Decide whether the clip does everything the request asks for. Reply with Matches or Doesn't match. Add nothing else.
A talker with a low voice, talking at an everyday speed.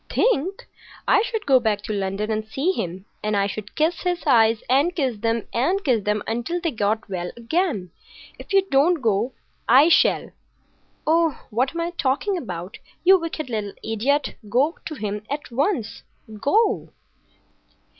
Doesn't match